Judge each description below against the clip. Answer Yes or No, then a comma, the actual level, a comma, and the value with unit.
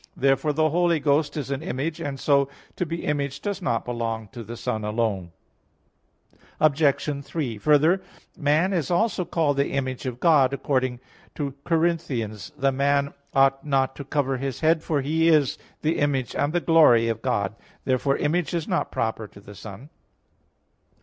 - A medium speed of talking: Yes, average, 175 wpm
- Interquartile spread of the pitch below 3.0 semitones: No, average, 3.8 semitones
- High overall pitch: No, medium, 140 Hz